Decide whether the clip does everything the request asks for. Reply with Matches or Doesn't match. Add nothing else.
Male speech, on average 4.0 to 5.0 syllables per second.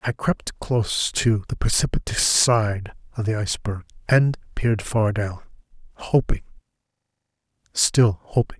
Matches